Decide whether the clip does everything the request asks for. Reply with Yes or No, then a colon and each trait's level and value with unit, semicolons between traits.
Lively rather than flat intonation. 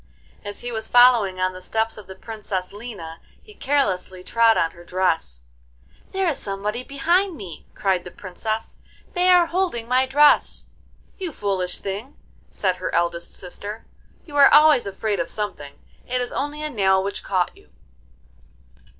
Yes: wide, 6.1 semitones